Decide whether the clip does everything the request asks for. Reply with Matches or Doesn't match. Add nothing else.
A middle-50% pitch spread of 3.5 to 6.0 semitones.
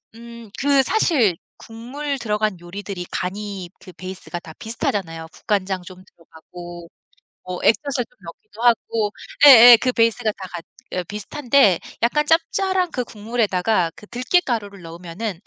Matches